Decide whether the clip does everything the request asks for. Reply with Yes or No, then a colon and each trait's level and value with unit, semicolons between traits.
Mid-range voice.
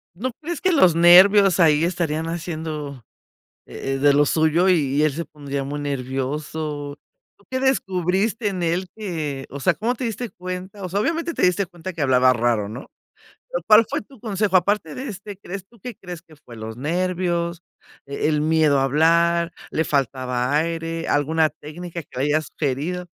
Yes: medium, 165 Hz